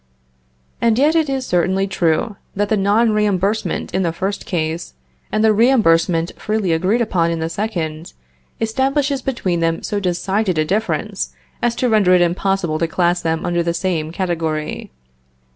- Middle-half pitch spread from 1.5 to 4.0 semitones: No, average, 4.6 semitones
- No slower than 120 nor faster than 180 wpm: Yes, average, 160 wpm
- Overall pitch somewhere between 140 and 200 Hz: Yes, high, 190 Hz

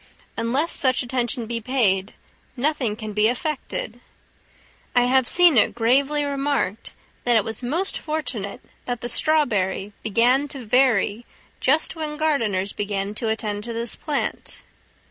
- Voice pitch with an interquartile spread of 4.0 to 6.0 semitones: Yes, average, 4.5 semitones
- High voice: Yes, high, 245 Hz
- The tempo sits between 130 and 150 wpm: Yes, average, 140 wpm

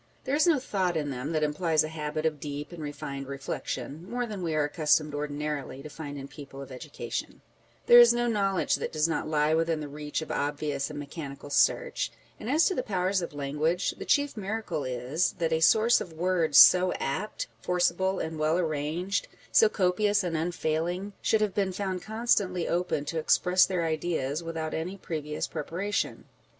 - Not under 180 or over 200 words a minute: Yes, average, 190 wpm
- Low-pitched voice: No, medium, 165 Hz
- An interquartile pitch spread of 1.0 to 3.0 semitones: No, average, 4.1 semitones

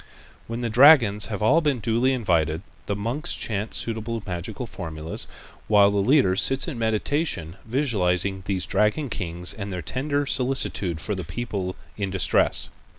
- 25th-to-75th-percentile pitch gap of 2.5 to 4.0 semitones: No, average, 5.1 semitones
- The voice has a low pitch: Yes, low, 105 Hz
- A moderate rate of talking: Yes, average, 150 wpm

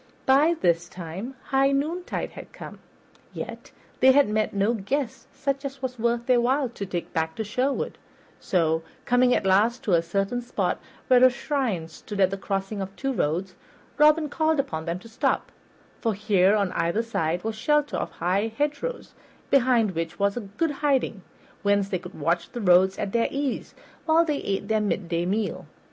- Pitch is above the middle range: Yes, high, 220 Hz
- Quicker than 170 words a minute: Yes, average, 180 wpm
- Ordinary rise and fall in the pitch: No, wide, 6.1 semitones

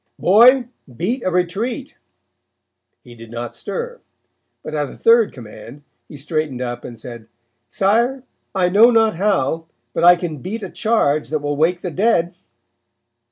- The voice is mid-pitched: Yes, medium, 175 Hz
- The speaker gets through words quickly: No, average, 155 wpm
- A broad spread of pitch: Yes, wide, 7.4 semitones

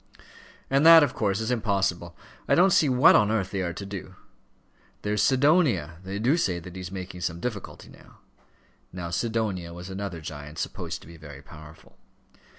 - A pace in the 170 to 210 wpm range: Yes, average, 175 wpm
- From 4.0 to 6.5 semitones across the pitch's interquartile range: Yes, average, 5.0 semitones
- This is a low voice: Yes, very low, 95 Hz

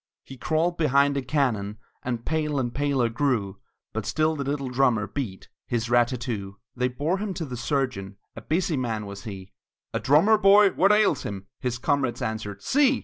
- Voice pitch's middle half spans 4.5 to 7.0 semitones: Yes, wide, 5.4 semitones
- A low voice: Yes, low, 130 Hz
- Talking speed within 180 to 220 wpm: Yes, average, 190 wpm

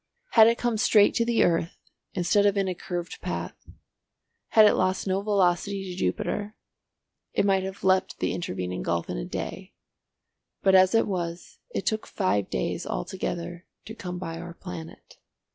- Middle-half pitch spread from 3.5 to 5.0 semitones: No, average, 2.9 semitones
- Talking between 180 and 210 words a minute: No, average, 170 wpm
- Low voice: No, medium, 185 Hz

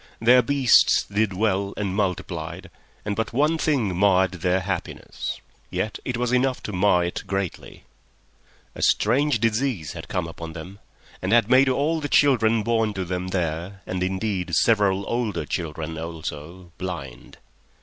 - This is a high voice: No, low, 100 Hz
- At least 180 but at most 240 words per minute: No, average, 145 wpm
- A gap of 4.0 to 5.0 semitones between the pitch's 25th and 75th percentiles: Yes, average, 4.3 semitones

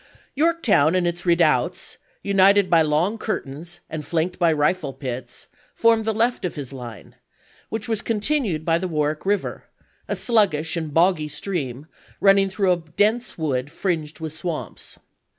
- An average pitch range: Yes, average, 4.9 semitones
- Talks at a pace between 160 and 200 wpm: No, average, 150 wpm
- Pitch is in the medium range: Yes, medium, 175 Hz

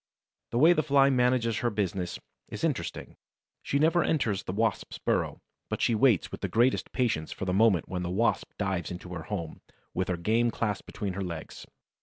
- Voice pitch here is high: No, low, 105 Hz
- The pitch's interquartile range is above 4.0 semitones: Yes, average, 5.2 semitones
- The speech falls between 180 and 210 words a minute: Yes, average, 195 wpm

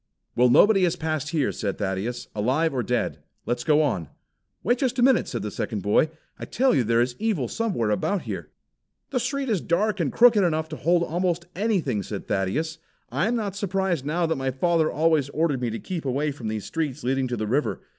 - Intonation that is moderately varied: No, wide, 7.1 semitones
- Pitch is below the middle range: No, medium, 155 Hz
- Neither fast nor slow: No, fast, 215 wpm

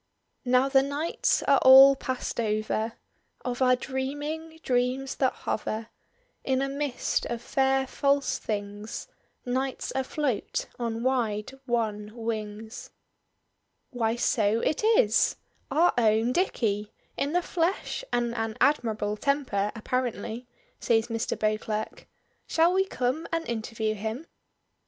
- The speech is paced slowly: Yes, slow, 120 wpm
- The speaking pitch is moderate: No, high, 245 Hz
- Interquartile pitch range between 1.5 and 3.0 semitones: No, average, 3.8 semitones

